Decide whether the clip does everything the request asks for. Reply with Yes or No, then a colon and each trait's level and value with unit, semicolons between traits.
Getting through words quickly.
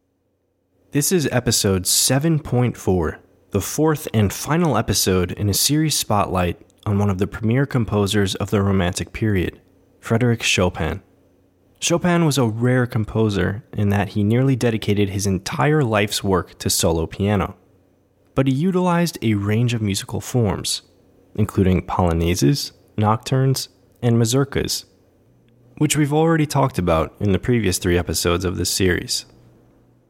No: slow, 135 wpm